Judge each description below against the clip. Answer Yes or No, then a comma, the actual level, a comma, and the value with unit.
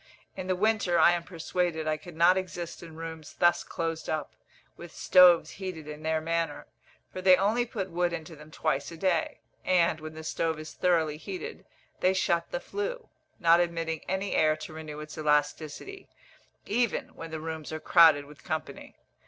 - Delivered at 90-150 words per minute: No, average, 180 wpm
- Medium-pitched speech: Yes, medium, 165 Hz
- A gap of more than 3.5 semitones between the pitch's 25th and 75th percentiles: No, narrow, 2.6 semitones